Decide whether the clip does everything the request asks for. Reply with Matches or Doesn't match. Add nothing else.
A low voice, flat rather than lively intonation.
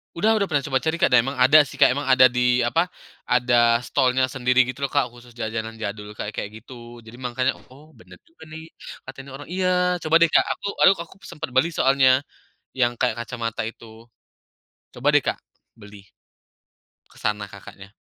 Doesn't match